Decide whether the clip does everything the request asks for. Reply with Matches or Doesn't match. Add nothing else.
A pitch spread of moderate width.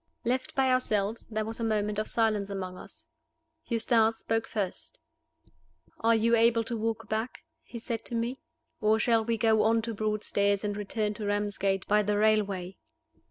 Doesn't match